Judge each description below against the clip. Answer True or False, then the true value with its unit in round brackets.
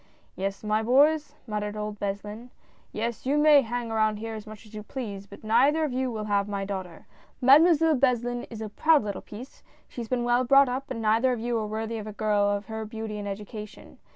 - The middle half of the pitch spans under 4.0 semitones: True (3.1 semitones)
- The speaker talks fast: True (230 wpm)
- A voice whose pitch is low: False (220 Hz)